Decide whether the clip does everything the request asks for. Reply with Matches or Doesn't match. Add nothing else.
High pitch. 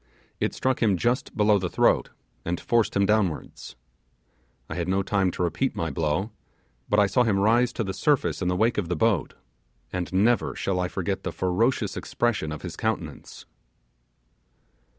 Doesn't match